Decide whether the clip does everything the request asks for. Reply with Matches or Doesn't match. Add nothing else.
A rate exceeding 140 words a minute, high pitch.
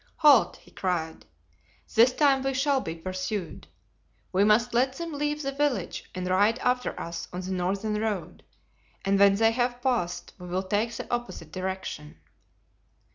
Matches